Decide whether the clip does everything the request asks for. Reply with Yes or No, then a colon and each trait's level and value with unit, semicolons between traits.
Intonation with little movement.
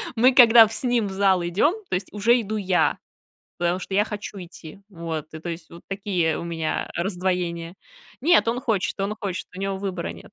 No: average, 3.7 semitones